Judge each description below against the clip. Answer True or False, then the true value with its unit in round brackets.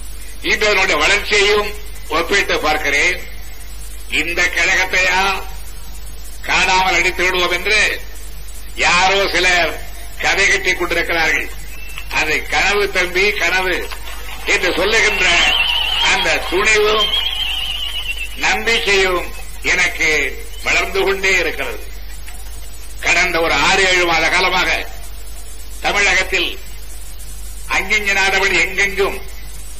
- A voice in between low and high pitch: True (175 Hz)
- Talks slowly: True (70 wpm)